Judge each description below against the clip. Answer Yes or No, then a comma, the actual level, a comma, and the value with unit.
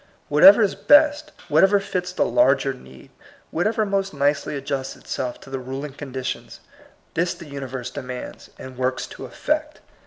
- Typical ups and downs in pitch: No, wide, 7.0 semitones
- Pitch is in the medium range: Yes, medium, 145 Hz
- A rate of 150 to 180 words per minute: Yes, average, 155 wpm